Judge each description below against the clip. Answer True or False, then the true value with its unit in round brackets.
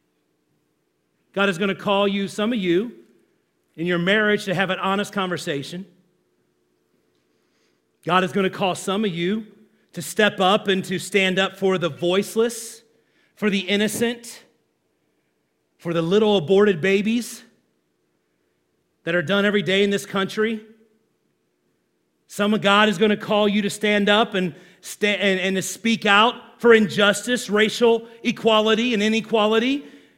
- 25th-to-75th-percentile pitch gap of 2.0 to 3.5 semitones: True (3.0 semitones)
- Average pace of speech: True (150 wpm)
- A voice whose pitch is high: True (200 Hz)